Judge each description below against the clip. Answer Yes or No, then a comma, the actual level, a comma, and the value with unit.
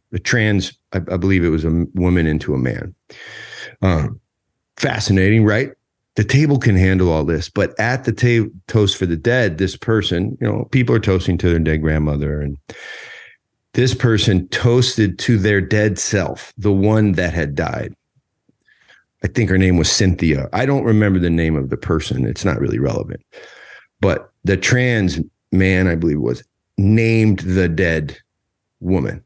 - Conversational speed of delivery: Yes, average, 170 wpm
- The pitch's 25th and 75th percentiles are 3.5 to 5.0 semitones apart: Yes, average, 4.2 semitones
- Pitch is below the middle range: Yes, very low, 95 Hz